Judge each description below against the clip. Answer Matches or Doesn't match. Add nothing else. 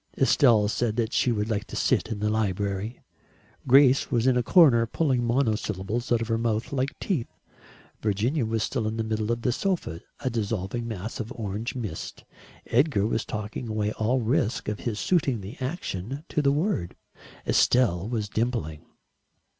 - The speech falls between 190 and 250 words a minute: Doesn't match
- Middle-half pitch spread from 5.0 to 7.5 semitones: Doesn't match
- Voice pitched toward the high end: Doesn't match